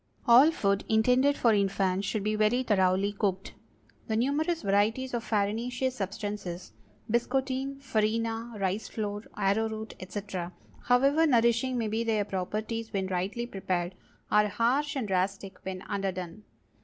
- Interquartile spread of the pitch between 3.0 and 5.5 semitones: Yes, average, 3.5 semitones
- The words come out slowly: Yes, slow, 130 wpm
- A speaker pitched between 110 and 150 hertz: No, high, 215 Hz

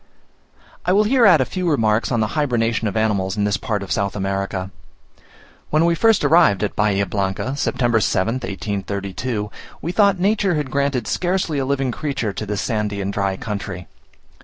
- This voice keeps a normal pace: Yes, average, 180 wpm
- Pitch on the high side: No, low, 115 Hz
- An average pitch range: No, wide, 6.9 semitones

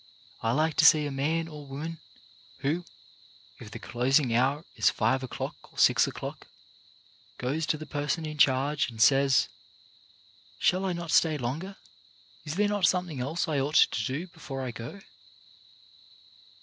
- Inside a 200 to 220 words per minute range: No, average, 160 wpm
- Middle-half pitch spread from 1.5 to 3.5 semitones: No, average, 3.9 semitones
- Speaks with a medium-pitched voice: Yes, medium, 145 Hz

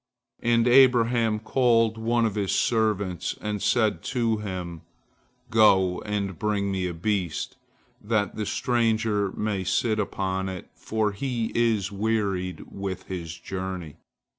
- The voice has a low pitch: Yes, low, 105 Hz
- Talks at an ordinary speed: No, slow, 130 wpm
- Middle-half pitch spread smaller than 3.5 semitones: Yes, average, 3.1 semitones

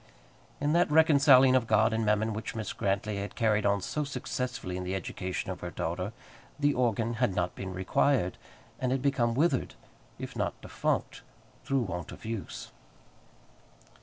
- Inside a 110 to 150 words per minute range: No, average, 165 wpm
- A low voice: Yes, low, 110 Hz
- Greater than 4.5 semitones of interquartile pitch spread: Yes, average, 5.1 semitones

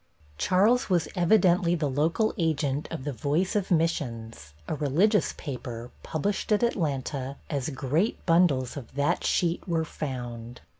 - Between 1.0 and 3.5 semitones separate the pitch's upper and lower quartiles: No, average, 5.1 semitones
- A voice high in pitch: No, medium, 155 Hz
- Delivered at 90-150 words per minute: Yes, average, 140 wpm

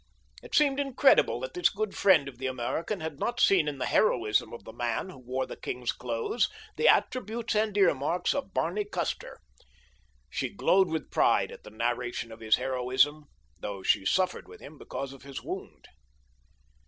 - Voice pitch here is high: No, medium, 145 Hz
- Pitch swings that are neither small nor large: No, wide, 8.4 semitones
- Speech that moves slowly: No, average, 180 wpm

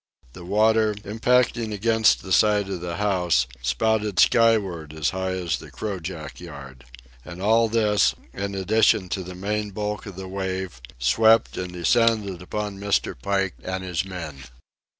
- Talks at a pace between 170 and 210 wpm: No, average, 150 wpm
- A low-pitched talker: Yes, very low, 95 Hz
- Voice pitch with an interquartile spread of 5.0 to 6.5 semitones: No, average, 3.0 semitones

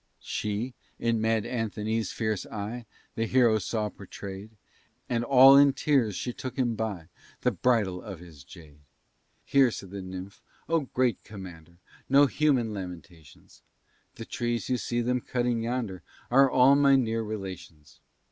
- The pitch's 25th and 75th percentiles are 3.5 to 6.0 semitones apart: Yes, average, 4.5 semitones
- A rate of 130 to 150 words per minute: Yes, average, 145 wpm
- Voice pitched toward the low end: Yes, low, 110 Hz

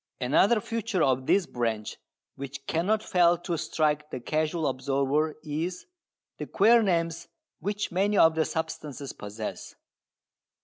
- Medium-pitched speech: Yes, medium, 160 Hz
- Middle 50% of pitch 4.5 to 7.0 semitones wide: Yes, average, 4.8 semitones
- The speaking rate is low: Yes, slow, 130 wpm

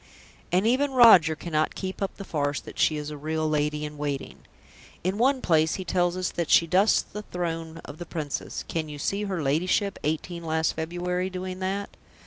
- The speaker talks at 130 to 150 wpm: No, average, 195 wpm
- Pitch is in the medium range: Yes, medium, 170 Hz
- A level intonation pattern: No, average, 3.3 semitones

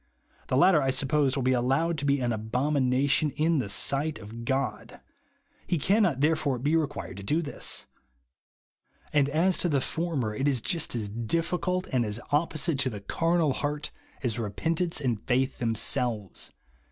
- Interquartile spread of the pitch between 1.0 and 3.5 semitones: No, average, 4.5 semitones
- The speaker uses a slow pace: No, average, 170 wpm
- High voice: No, medium, 140 Hz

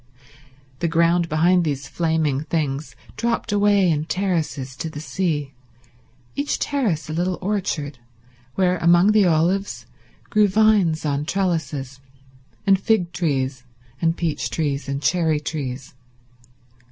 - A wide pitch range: No, average, 4.2 semitones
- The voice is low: No, medium, 165 Hz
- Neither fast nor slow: No, slow, 125 wpm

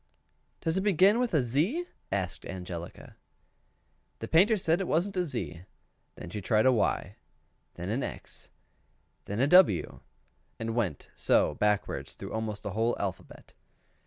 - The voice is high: No, low, 115 Hz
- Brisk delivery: No, average, 150 wpm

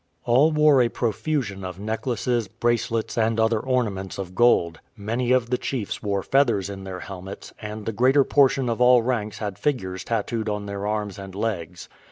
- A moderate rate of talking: Yes, average, 180 wpm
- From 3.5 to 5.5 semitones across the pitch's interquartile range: Yes, average, 3.8 semitones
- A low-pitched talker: Yes, low, 110 Hz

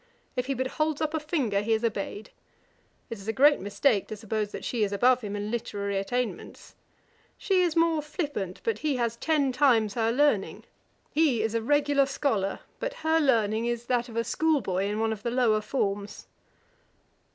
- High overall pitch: Yes, high, 235 Hz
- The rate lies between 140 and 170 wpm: No, average, 195 wpm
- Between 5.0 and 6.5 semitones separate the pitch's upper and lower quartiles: Yes, wide, 5.5 semitones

